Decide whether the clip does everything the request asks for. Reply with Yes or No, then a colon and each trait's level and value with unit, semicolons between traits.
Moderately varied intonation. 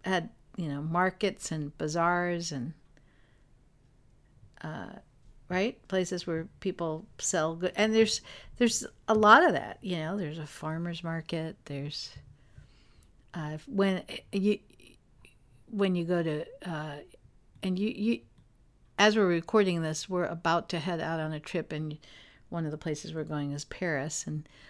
Yes: average, 3.8 semitones